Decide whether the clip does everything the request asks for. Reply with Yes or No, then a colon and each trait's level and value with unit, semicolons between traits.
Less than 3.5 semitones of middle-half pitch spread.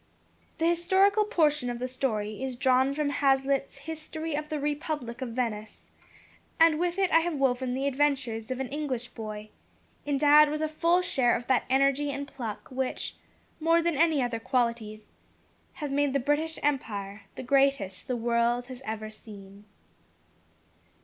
No: average, 4.1 semitones